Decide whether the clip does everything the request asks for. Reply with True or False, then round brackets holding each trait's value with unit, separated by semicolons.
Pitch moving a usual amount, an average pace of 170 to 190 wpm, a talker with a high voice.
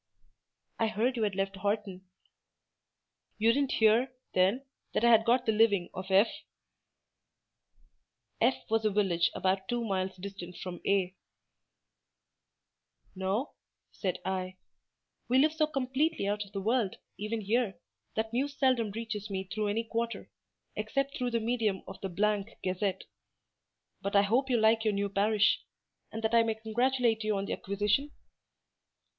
False (3.1 semitones; 150 wpm; 215 Hz)